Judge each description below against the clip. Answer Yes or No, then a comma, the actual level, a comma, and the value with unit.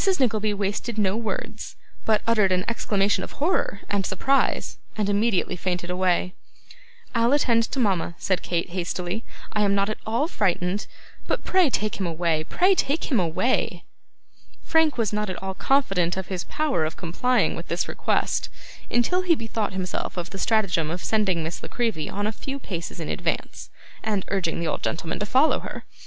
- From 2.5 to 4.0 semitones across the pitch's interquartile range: No, average, 4.4 semitones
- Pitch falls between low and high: No, high, 205 Hz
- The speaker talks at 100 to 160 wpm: No, average, 180 wpm